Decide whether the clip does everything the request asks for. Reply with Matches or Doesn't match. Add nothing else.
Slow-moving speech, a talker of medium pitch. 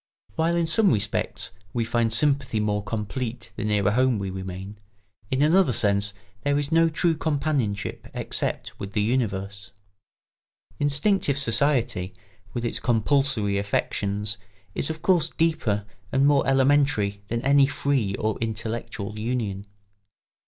Doesn't match